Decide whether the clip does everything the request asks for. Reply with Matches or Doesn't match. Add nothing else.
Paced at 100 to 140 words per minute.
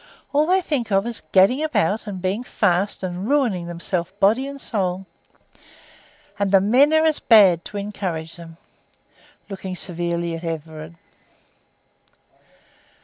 Matches